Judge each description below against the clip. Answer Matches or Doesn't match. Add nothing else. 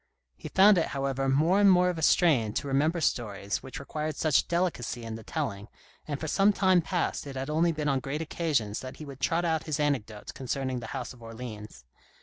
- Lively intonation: Doesn't match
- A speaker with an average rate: Doesn't match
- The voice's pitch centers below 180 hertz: Matches